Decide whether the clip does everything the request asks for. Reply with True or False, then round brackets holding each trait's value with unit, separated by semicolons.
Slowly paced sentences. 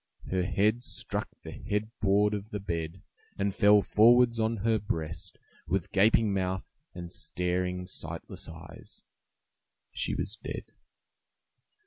True (125 wpm)